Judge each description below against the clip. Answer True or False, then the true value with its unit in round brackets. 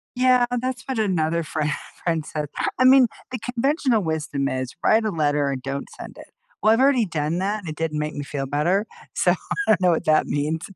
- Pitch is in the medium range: True (165 Hz)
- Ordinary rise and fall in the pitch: False (7.1 semitones)